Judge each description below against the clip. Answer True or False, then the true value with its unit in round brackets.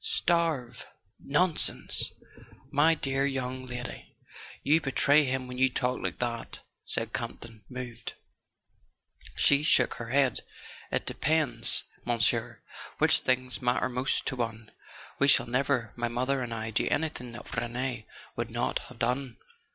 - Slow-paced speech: True (130 wpm)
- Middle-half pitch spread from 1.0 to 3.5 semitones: True (2.6 semitones)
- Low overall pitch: True (125 Hz)